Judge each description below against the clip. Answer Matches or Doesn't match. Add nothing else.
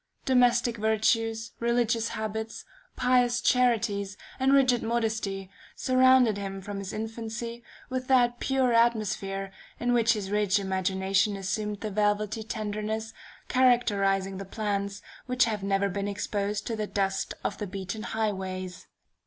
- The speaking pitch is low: Doesn't match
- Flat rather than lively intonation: Doesn't match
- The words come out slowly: Matches